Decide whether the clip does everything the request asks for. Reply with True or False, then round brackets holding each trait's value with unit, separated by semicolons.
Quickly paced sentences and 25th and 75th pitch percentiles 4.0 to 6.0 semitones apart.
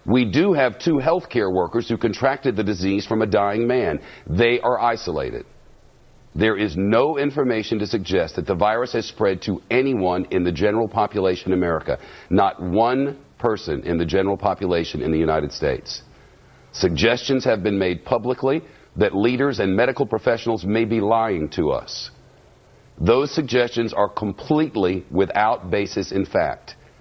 False (160 wpm; 4.5 semitones)